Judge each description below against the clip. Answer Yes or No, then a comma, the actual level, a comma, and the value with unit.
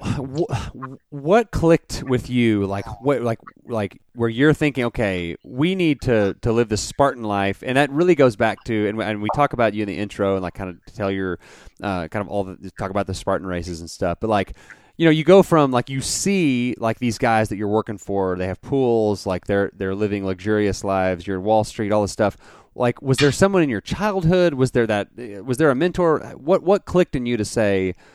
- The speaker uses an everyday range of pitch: No, wide, 5.8 semitones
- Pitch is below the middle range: Yes, low, 110 Hz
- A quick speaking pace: Yes, fast, 230 wpm